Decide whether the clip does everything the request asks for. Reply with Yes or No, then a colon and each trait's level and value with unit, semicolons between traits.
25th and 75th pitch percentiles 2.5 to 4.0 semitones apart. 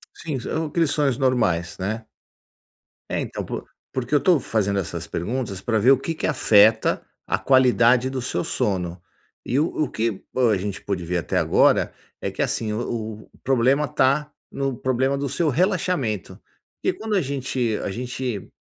No: average, 4.5 semitones